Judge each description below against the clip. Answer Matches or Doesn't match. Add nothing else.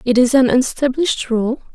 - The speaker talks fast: Doesn't match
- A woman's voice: Matches